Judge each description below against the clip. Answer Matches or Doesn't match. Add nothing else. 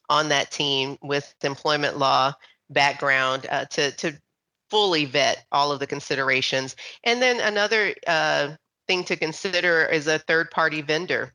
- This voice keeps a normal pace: Matches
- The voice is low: Doesn't match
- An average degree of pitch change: Matches